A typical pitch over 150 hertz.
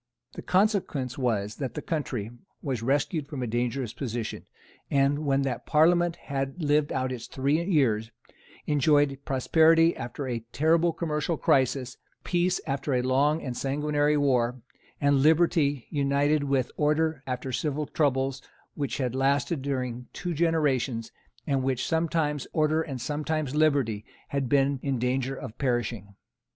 No: medium, 140 Hz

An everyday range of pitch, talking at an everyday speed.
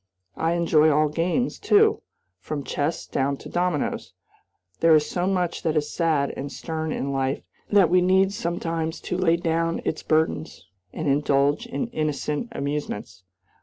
Yes: average, 3.1 semitones; average, 155 wpm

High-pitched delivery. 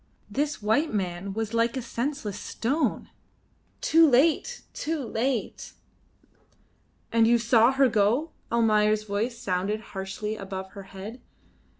Yes: high, 225 Hz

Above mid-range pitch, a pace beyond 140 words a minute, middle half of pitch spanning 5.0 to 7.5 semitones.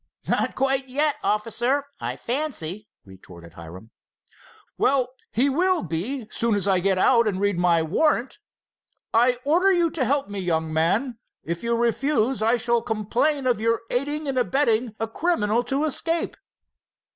Yes: high, 235 Hz; average, 155 wpm; wide, 5.5 semitones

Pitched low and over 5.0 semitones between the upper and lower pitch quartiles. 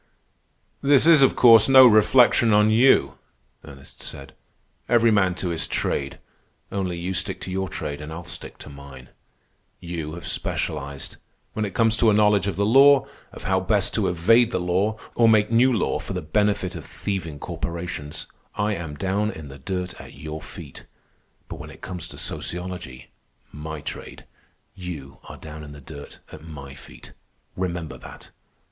Yes: very low, 90 Hz; wide, 5.6 semitones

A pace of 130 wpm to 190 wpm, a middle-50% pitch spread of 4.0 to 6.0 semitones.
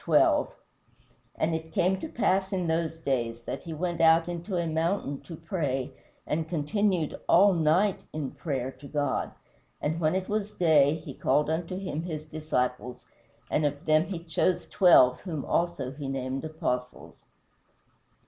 No: average, 160 wpm; average, 3.5 semitones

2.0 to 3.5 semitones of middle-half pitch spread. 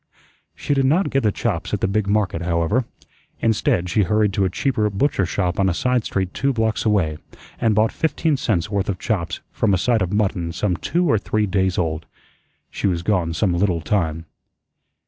No: average, 3.9 semitones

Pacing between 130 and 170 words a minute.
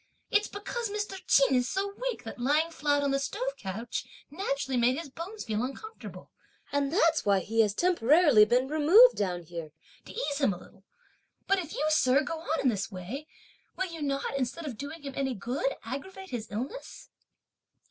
No: average, 190 wpm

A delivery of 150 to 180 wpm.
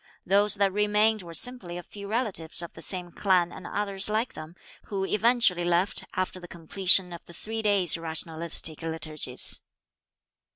Yes: average, 160 wpm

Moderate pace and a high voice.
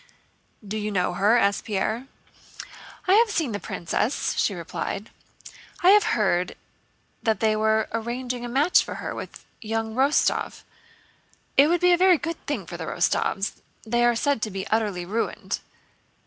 Yes: average, 160 wpm; high, 225 Hz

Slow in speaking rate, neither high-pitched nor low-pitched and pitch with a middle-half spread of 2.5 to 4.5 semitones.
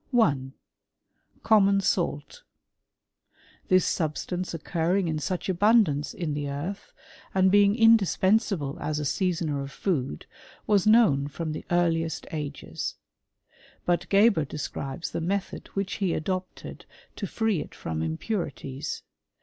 No: slow, 120 wpm; medium, 175 Hz; average, 5.1 semitones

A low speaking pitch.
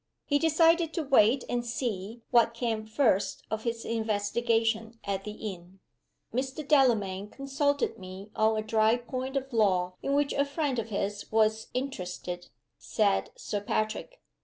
No: high, 225 Hz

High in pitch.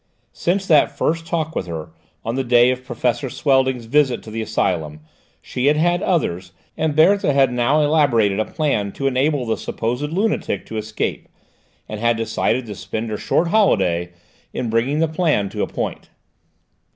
No: low, 125 Hz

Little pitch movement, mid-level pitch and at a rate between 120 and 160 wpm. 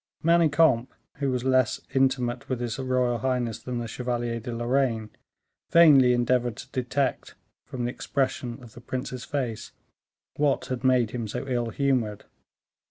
No: narrow, 1.8 semitones; low, 125 Hz; average, 150 wpm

